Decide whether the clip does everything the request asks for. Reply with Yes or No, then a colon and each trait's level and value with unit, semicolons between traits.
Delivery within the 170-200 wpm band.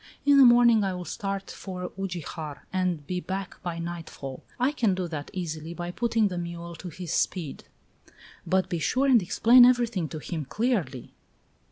Yes: average, 175 wpm